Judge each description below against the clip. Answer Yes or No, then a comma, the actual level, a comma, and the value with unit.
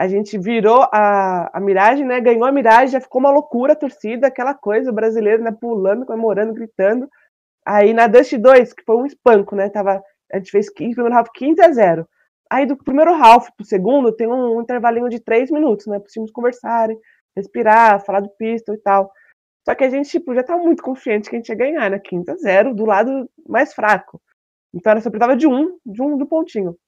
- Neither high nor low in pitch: No, high, 230 Hz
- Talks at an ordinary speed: No, fast, 225 wpm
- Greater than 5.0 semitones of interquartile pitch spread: No, average, 4.1 semitones